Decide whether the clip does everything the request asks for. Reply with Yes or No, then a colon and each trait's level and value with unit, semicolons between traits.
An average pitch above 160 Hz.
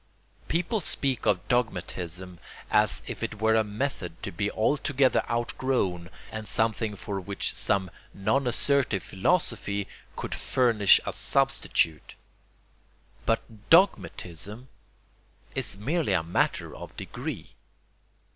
No: low, 105 Hz